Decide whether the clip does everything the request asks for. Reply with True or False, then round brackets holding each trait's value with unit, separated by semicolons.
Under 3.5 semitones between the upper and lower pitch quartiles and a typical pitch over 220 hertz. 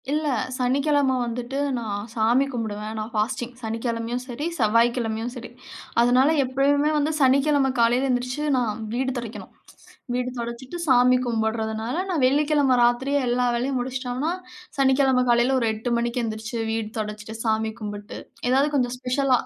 True (2.7 semitones; 245 Hz)